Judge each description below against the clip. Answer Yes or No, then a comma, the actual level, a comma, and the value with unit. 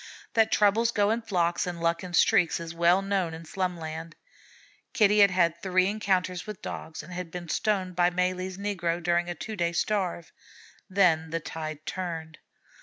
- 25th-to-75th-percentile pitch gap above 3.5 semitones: No, average, 2.7 semitones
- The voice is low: No, medium, 180 Hz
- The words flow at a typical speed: Yes, average, 175 wpm